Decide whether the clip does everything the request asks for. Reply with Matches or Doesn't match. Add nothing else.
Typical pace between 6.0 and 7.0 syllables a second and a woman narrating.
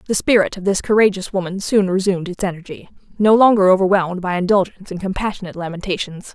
Matches